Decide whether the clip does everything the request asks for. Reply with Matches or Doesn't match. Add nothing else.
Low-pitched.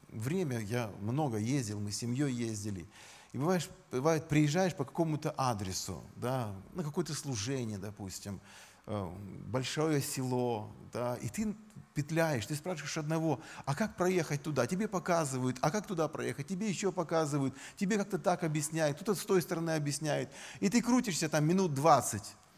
Doesn't match